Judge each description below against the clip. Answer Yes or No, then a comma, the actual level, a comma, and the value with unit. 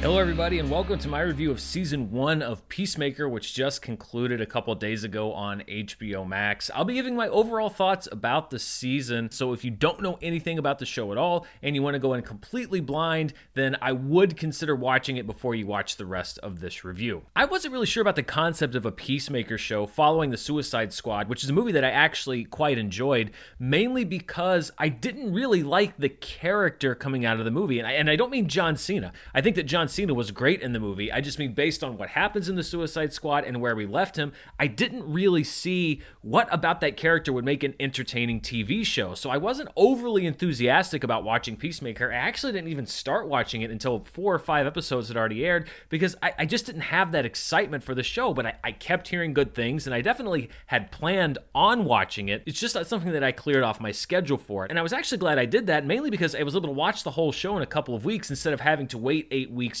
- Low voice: No, medium, 145 Hz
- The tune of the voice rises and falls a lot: Yes, wide, 6.3 semitones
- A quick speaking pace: Yes, fast, 240 wpm